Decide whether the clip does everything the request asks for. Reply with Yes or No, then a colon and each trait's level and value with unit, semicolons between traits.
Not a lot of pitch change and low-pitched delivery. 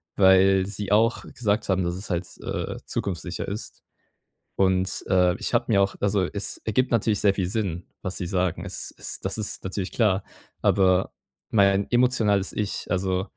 Yes: narrow, 1.9 semitones; very low, 95 Hz